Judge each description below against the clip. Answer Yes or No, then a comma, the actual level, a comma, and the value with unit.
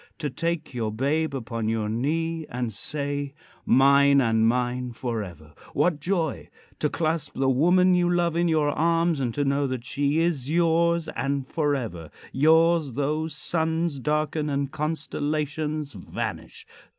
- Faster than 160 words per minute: No, average, 140 wpm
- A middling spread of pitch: Yes, average, 3.7 semitones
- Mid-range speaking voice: Yes, medium, 145 Hz